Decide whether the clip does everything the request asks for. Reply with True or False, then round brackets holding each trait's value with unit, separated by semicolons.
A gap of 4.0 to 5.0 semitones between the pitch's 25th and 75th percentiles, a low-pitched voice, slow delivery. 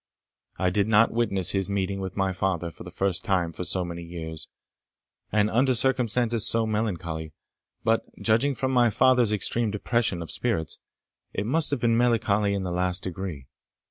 False (4.3 semitones; 100 Hz; 175 wpm)